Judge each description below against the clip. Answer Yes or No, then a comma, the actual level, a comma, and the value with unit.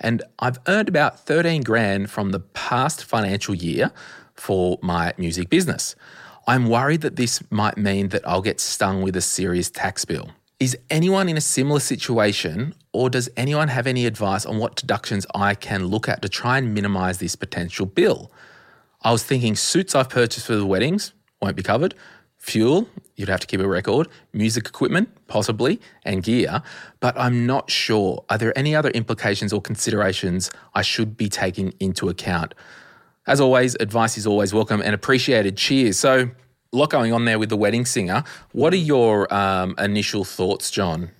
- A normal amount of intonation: Yes, average, 4.4 semitones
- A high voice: No, low, 110 Hz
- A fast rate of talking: No, average, 180 wpm